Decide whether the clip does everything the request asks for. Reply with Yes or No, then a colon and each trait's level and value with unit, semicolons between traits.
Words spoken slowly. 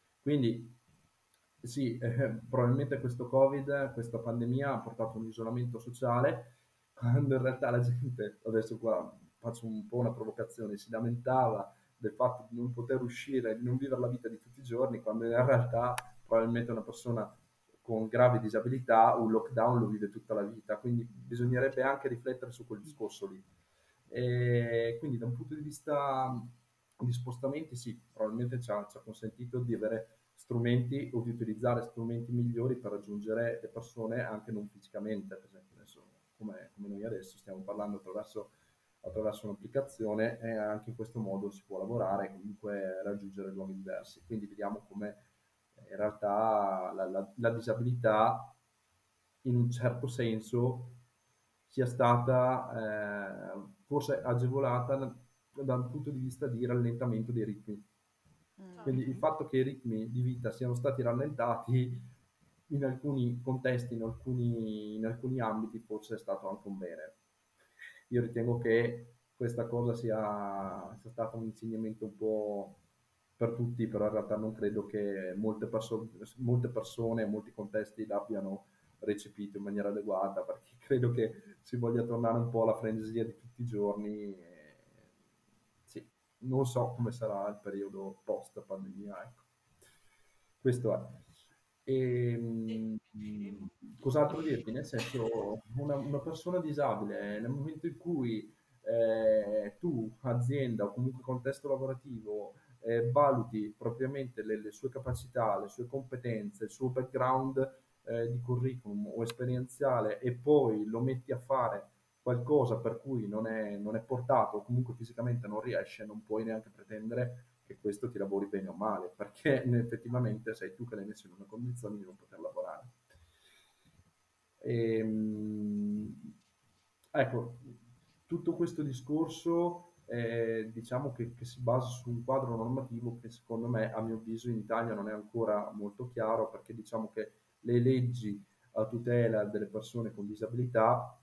No: average, 150 wpm